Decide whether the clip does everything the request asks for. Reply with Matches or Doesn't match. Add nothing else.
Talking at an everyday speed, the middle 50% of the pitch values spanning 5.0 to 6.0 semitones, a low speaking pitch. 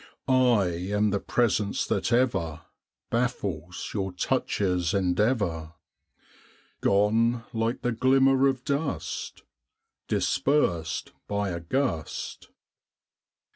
Doesn't match